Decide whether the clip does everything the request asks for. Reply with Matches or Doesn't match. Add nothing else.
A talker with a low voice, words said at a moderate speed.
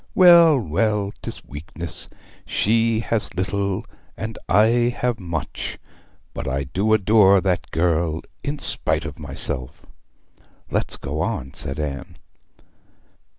Doesn't match